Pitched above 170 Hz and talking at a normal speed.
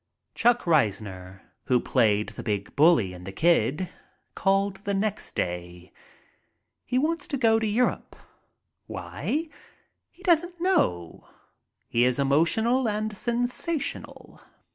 No: medium, 185 Hz; slow, 120 wpm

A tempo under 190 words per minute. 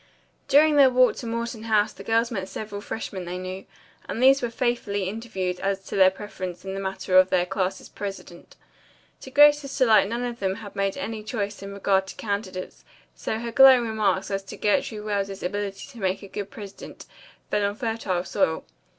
No: average, 195 wpm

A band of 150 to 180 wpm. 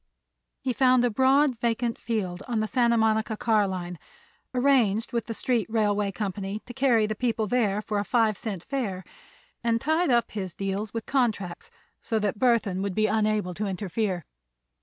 Yes: average, 175 wpm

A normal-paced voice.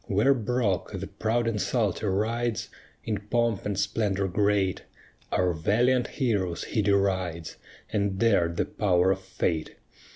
No: slow, 130 wpm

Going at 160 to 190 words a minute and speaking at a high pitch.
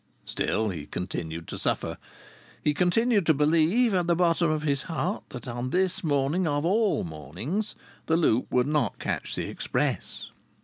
No: average, 165 wpm; medium, 155 Hz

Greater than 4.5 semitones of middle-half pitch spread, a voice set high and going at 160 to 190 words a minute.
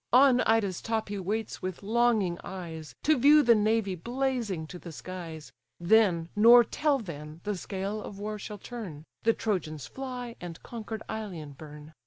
Yes: average, 5.1 semitones; high, 210 Hz; average, 165 wpm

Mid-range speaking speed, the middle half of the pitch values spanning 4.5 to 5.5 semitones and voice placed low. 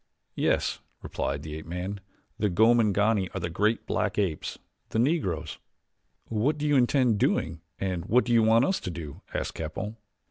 Yes: average, 170 wpm; average, 5.2 semitones; low, 105 Hz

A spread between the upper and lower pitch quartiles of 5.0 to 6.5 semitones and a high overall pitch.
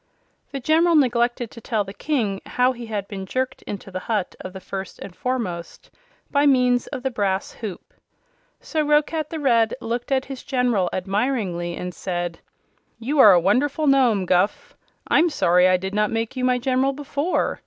Yes: wide, 5.6 semitones; high, 235 Hz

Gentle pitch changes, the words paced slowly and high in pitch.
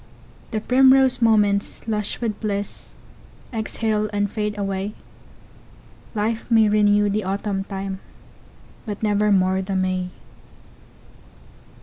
Yes: narrow, 1.7 semitones; slow, 85 wpm; high, 210 Hz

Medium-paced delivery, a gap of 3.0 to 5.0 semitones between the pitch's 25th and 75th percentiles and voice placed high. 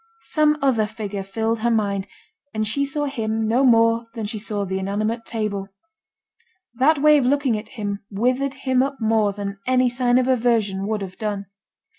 Yes: average, 180 wpm; average, 3.7 semitones; high, 225 Hz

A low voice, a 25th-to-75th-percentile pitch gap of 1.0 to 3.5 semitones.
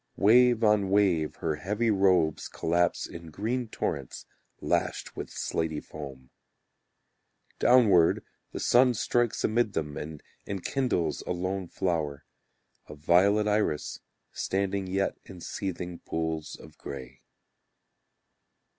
No: very low, 95 Hz; average, 4.8 semitones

